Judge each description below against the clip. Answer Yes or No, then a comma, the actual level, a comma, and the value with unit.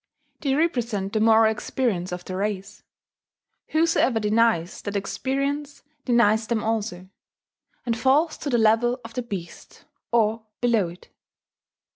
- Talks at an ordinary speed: No, slow, 130 wpm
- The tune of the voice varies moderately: Yes, average, 3.4 semitones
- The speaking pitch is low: No, high, 225 Hz